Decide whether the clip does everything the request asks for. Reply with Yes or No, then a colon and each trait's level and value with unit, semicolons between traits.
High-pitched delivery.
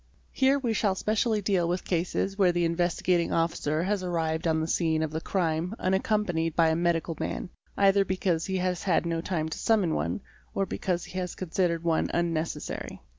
No: medium, 175 Hz